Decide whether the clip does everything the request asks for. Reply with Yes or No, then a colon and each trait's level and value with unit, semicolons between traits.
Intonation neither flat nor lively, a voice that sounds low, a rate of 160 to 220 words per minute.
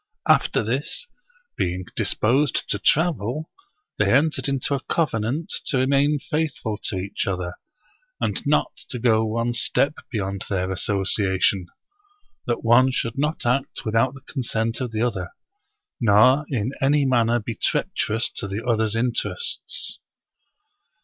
No: average, 4.4 semitones; low, 120 Hz; slow, 135 wpm